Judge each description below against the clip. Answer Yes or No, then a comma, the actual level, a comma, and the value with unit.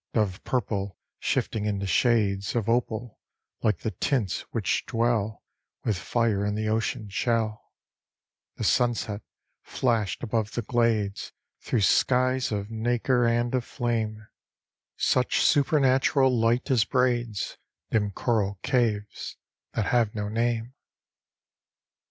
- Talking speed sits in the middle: No, slow, 115 wpm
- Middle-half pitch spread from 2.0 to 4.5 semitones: Yes, narrow, 2.5 semitones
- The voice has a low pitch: Yes, low, 115 Hz